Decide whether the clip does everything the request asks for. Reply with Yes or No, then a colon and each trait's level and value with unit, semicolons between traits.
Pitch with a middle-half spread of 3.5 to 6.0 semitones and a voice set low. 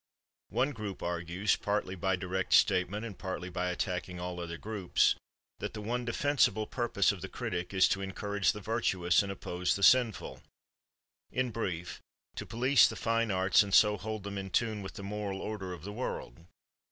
No: average, 3.1 semitones; low, 100 Hz